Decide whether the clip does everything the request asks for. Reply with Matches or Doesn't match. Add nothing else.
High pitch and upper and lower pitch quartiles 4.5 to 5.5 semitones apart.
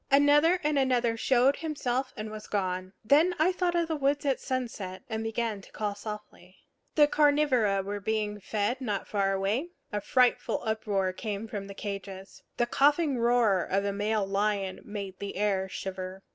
Matches